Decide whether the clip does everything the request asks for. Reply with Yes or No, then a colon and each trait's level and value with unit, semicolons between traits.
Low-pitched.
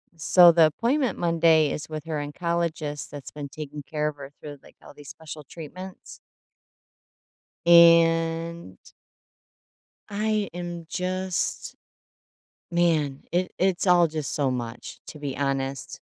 No: medium, 165 Hz